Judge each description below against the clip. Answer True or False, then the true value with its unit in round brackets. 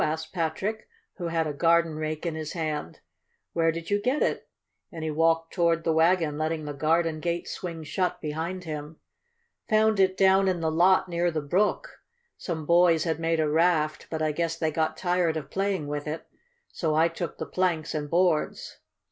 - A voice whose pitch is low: False (165 Hz)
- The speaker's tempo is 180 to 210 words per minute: True (190 wpm)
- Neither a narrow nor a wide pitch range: False (2.1 semitones)